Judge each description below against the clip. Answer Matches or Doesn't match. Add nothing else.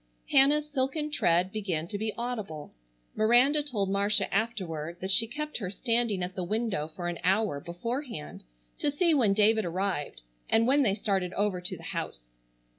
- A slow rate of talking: Doesn't match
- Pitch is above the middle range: Matches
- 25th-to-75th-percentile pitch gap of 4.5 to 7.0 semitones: Matches